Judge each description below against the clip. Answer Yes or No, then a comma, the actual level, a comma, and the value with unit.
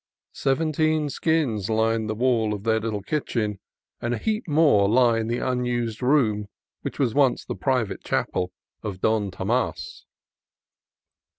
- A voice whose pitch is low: Yes, low, 115 Hz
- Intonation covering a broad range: No, average, 4.2 semitones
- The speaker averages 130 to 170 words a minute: Yes, average, 140 wpm